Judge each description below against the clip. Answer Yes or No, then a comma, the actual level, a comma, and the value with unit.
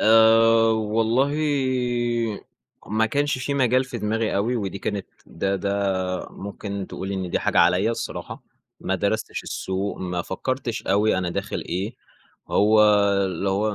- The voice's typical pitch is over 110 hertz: No, low, 105 Hz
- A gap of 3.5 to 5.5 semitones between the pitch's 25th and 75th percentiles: No, average, 2.7 semitones